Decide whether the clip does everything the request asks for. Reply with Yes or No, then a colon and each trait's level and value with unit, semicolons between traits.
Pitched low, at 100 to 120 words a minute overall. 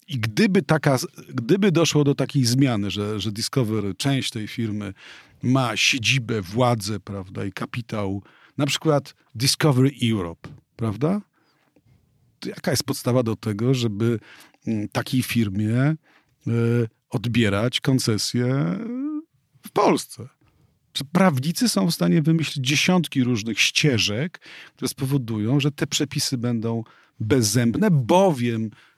Yes: low, 130 Hz; average, 115 wpm